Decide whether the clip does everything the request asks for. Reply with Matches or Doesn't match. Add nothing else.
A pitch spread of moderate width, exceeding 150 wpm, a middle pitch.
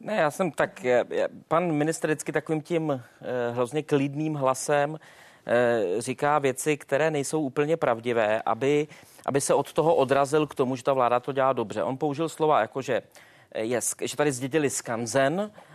Matches